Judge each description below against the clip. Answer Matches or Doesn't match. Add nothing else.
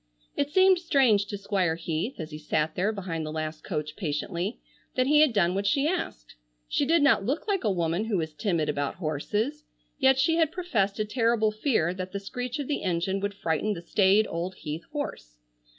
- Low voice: Doesn't match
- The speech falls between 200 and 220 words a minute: Matches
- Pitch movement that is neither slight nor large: Doesn't match